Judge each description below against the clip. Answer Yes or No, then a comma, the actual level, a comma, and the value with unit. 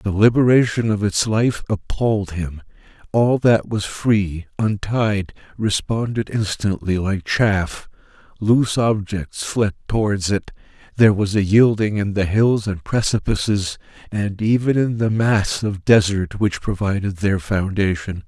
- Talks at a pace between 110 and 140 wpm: Yes, slow, 135 wpm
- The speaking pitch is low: Yes, low, 105 Hz